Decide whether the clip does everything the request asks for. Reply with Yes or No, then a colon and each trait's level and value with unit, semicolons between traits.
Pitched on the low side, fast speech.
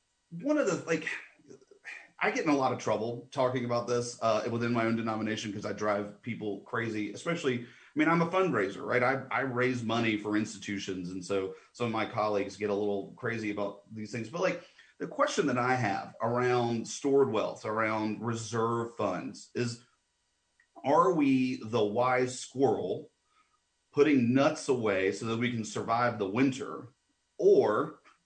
No: low, 115 Hz; average, 170 wpm